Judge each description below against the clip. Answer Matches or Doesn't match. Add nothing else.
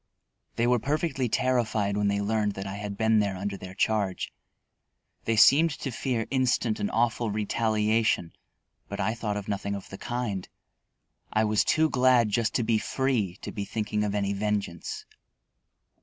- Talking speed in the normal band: Matches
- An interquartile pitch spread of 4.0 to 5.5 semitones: Doesn't match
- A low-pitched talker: Matches